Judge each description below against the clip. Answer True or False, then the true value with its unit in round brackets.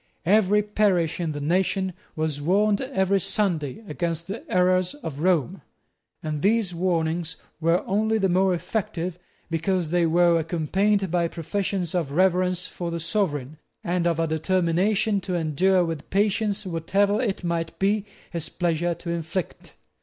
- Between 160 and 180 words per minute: False (145 wpm)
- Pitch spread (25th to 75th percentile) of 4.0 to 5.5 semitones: False (3.0 semitones)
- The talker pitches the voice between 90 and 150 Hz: False (180 Hz)